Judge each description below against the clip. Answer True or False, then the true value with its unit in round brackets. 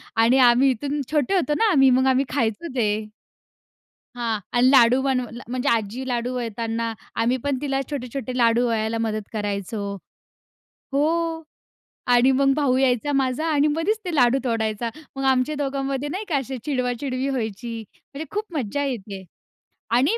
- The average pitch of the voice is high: True (255 Hz)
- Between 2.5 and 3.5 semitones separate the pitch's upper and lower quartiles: True (3.2 semitones)